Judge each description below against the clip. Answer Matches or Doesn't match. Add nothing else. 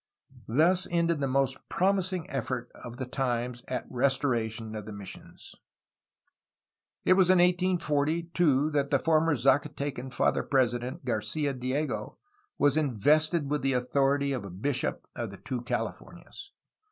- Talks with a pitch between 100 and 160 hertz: Matches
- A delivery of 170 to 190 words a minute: Doesn't match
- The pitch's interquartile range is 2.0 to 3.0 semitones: Doesn't match